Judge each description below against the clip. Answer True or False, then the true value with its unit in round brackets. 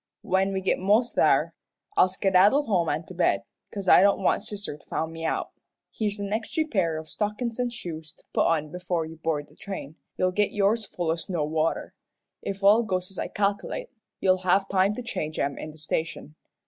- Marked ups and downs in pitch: False (4.1 semitones)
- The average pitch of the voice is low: False (185 Hz)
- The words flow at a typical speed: False (210 wpm)